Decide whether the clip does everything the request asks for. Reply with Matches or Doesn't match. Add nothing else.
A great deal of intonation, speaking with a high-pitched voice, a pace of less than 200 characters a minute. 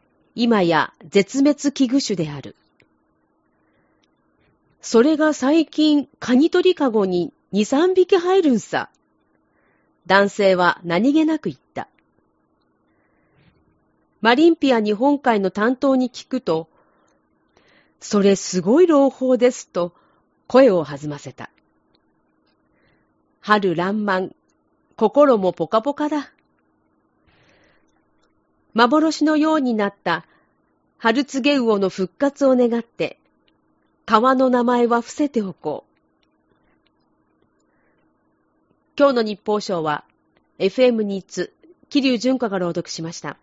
Matches